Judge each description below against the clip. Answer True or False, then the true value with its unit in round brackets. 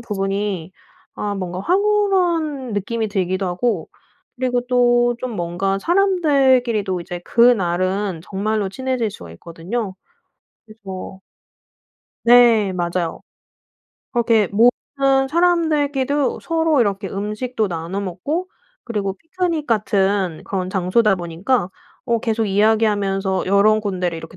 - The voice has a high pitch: True (210 Hz)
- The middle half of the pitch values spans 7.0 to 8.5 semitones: False (5.1 semitones)